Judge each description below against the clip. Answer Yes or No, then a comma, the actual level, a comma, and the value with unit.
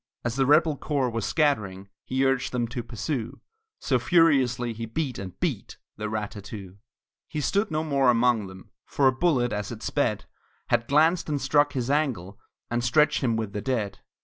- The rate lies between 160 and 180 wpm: No, average, 190 wpm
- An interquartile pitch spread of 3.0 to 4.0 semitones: No, average, 4.8 semitones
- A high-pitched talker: No, low, 125 Hz